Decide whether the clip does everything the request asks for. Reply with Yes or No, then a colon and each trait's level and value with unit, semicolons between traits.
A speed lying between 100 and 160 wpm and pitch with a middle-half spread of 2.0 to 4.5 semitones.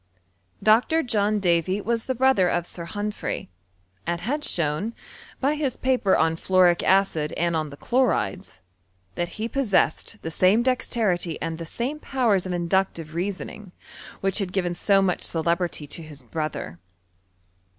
No: average, 150 wpm; average, 5.0 semitones